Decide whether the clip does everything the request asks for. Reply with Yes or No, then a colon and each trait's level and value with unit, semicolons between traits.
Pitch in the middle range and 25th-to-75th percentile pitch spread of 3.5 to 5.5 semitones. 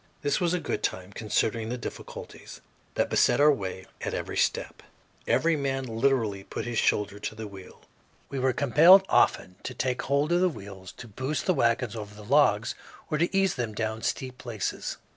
No: low, 120 Hz; average, 5.2 semitones